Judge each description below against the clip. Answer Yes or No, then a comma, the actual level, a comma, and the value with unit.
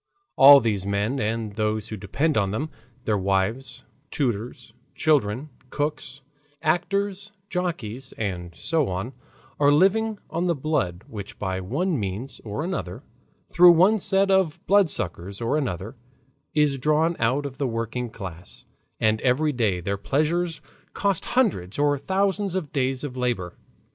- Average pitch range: No, wide, 7.5 semitones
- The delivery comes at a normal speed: Yes, average, 145 wpm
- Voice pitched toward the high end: No, low, 135 Hz